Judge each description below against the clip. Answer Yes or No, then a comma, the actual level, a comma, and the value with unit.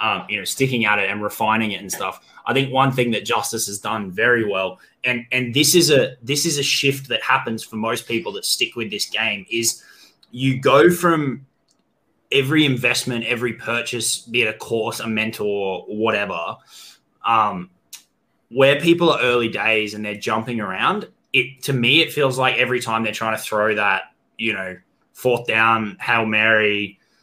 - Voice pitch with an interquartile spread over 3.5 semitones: No, average, 3.2 semitones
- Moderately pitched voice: No, low, 115 Hz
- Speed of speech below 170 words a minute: No, average, 185 wpm